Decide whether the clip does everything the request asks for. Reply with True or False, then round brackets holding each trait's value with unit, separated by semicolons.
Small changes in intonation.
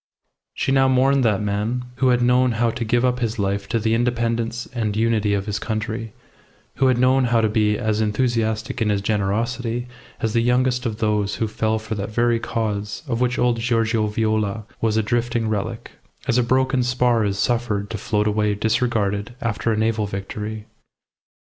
True (2.3 semitones)